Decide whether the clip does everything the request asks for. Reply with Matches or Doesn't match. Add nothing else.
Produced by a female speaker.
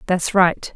Matches